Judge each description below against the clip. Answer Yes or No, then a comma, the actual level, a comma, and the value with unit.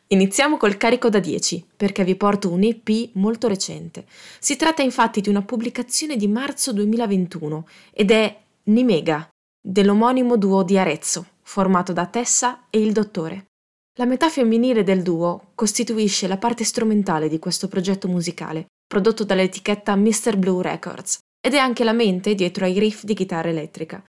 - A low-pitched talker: No, high, 205 Hz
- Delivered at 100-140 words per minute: No, average, 155 wpm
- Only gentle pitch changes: No, average, 3.8 semitones